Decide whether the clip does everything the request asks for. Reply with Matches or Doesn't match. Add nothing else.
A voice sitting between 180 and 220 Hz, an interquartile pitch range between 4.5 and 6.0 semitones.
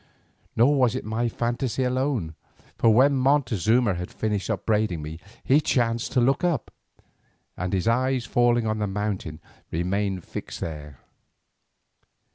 Doesn't match